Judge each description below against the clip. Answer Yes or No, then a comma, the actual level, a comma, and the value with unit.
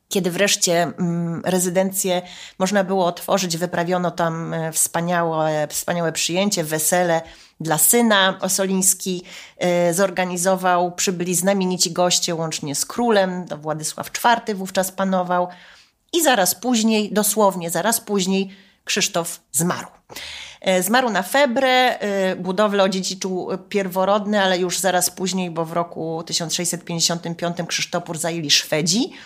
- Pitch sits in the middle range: Yes, medium, 180 Hz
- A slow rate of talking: Yes, slow, 105 wpm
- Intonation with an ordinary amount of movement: No, narrow, 2.3 semitones